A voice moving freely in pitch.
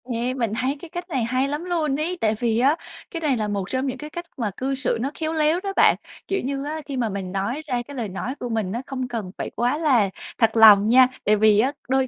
No: average, 4.8 semitones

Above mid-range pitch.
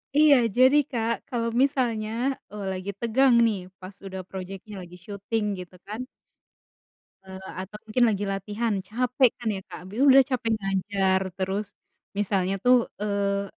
Yes: high, 210 Hz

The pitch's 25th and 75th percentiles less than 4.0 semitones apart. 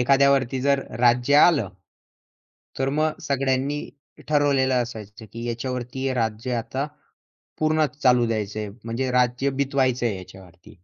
Yes: average, 2.9 semitones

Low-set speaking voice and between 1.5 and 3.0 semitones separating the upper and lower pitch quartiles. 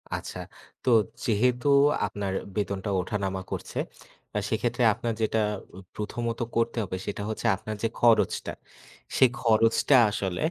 Yes: low, 110 Hz; narrow, 2.6 semitones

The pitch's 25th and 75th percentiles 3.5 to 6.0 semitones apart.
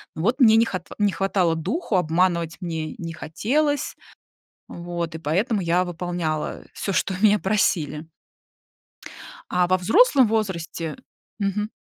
Yes: average, 4.1 semitones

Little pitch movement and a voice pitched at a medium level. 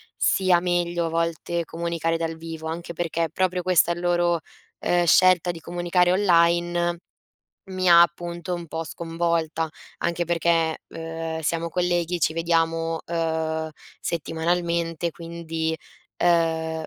Yes: narrow, 1.1 semitones; medium, 170 Hz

